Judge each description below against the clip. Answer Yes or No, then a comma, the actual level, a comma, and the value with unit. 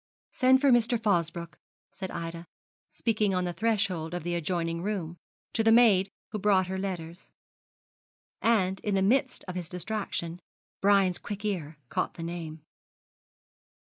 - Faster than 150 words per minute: No, average, 145 wpm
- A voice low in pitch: No, high, 190 Hz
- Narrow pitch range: No, average, 3.8 semitones